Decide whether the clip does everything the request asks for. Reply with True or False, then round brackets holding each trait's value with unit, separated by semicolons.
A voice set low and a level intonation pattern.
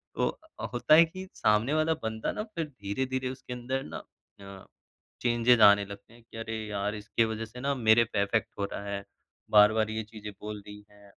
False (110 Hz; 3.3 semitones)